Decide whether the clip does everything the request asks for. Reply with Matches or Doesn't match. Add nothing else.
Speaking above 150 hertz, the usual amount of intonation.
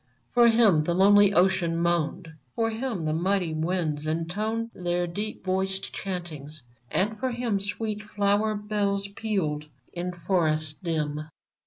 Matches